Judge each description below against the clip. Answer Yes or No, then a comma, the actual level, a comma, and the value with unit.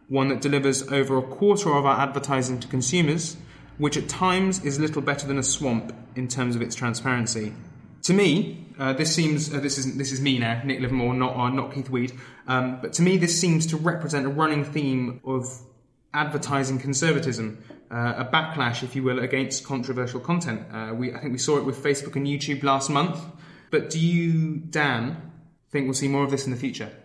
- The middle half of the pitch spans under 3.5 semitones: Yes, average, 2.8 semitones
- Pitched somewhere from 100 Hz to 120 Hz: No, low, 135 Hz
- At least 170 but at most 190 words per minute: No, fast, 205 wpm